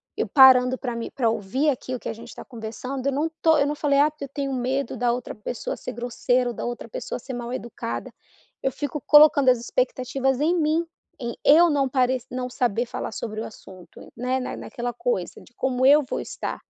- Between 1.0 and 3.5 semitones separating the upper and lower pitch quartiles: Yes, average, 2.7 semitones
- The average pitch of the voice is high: Yes, very high, 255 Hz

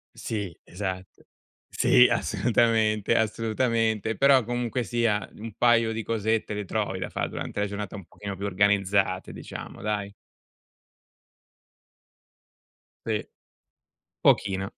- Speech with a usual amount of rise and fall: No, narrow, 2.3 semitones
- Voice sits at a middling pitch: No, low, 105 Hz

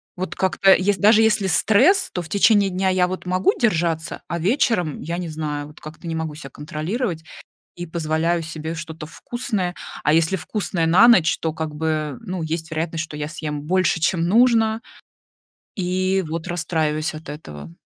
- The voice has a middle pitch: Yes, medium, 170 Hz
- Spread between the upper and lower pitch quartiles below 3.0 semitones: No, average, 3.3 semitones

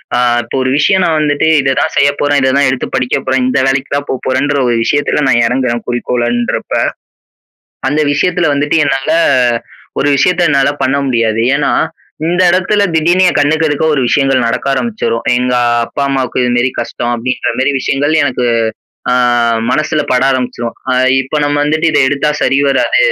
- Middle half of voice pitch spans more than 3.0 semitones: No, average, 2.7 semitones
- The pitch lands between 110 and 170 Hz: Yes, low, 135 Hz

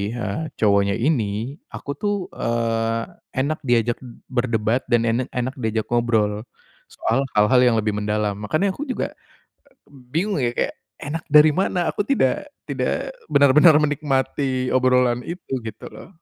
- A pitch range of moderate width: Yes, average, 4.5 semitones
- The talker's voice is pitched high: No, low, 125 Hz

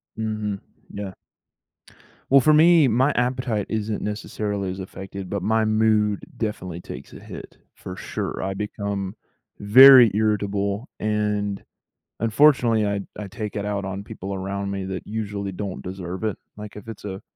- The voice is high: No, low, 105 Hz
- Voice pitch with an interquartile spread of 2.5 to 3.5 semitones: No, narrow, 2.0 semitones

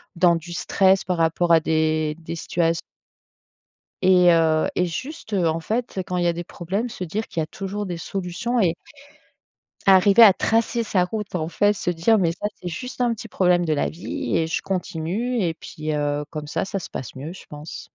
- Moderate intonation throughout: Yes, average, 3.6 semitones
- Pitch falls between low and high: Yes, medium, 175 Hz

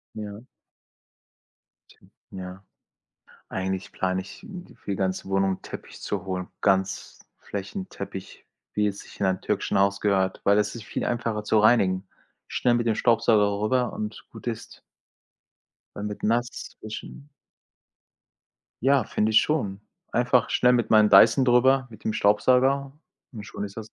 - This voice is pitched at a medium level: No, low, 105 Hz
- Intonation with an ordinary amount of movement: Yes, average, 3.6 semitones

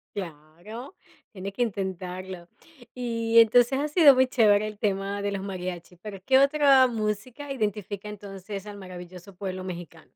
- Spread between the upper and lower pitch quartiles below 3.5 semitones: No, average, 4.0 semitones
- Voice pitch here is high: Yes, high, 205 Hz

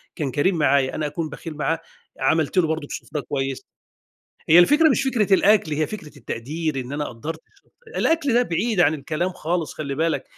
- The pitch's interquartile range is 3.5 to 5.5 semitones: Yes, average, 4.0 semitones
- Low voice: No, medium, 160 Hz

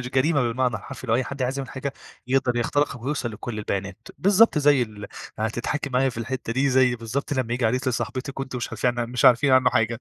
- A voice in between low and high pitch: No, low, 125 Hz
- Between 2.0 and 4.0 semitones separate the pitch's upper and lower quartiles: Yes, narrow, 2.4 semitones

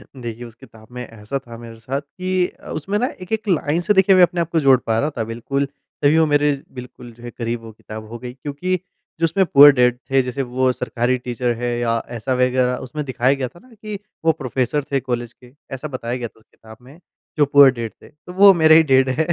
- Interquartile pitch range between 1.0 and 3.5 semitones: No, average, 4.6 semitones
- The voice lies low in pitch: Yes, low, 130 Hz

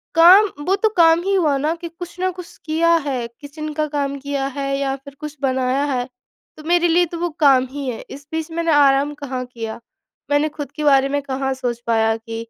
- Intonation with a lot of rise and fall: No, average, 3.6 semitones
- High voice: Yes, very high, 285 Hz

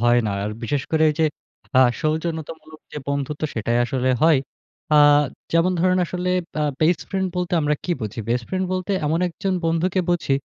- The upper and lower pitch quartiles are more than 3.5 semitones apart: Yes, average, 4.0 semitones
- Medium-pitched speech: Yes, medium, 160 Hz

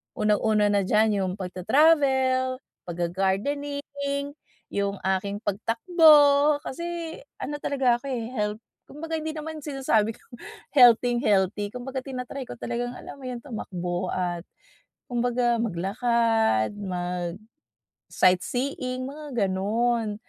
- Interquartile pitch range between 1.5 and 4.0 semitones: No, average, 5.3 semitones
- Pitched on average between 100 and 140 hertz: No, high, 240 Hz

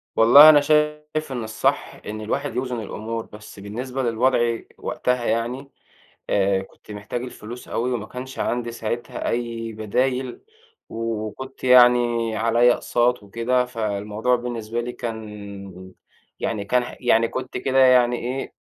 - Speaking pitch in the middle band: No, low, 120 Hz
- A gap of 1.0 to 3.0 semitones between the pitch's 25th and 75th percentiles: Yes, narrow, 2.5 semitones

